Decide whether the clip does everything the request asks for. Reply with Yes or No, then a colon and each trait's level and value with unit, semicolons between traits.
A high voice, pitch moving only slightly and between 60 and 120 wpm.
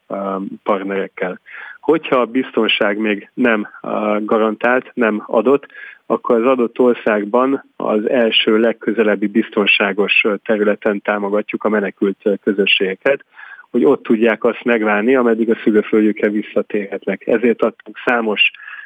No: low, 110 Hz; narrow, 2.1 semitones; average, 110 wpm